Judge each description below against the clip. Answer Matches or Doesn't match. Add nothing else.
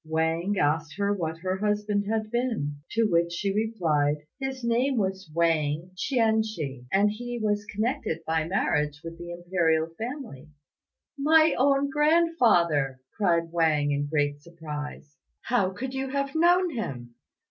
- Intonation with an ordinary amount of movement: Doesn't match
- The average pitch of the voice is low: Doesn't match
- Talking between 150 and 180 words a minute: Doesn't match